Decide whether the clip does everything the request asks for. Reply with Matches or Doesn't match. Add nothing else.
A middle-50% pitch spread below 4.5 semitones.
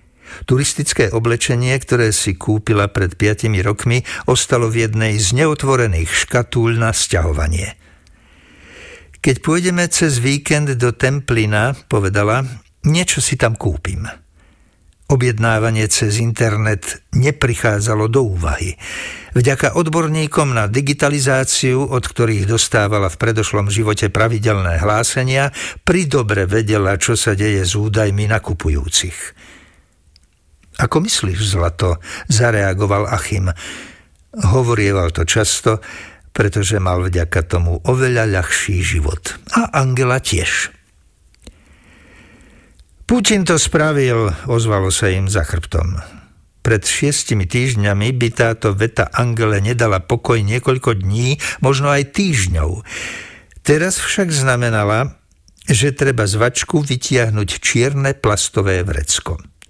Doesn't match